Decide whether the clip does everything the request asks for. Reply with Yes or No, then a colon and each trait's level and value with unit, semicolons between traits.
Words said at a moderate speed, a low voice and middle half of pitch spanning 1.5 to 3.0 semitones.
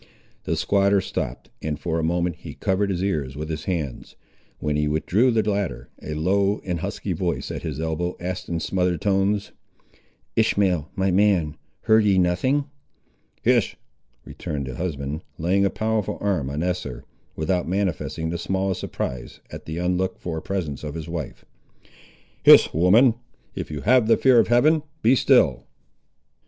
No: average, 160 wpm; very low, 90 Hz; average, 4.1 semitones